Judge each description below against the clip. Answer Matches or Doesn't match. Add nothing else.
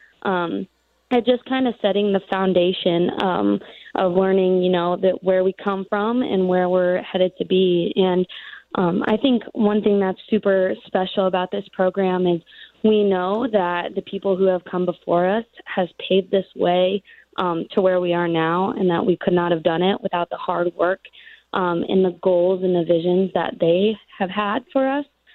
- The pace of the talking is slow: Doesn't match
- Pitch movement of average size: Doesn't match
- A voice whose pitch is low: Doesn't match